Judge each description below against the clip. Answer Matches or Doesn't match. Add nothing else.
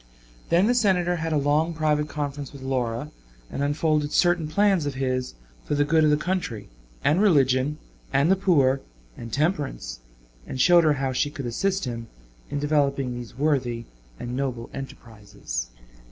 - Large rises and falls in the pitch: Doesn't match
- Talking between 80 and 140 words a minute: Doesn't match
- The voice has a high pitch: Doesn't match